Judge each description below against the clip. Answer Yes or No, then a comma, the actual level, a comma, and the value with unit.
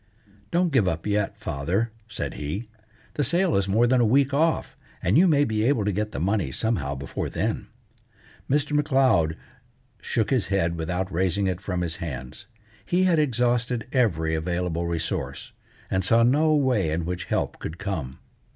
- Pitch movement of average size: No, wide, 7.2 semitones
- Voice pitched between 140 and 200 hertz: No, low, 105 Hz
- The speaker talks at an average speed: Yes, average, 170 wpm